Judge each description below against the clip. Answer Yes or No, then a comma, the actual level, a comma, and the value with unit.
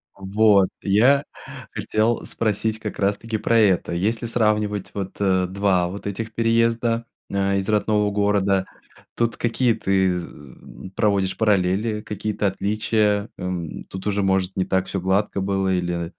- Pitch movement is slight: Yes, narrow, 2.3 semitones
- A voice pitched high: No, low, 100 Hz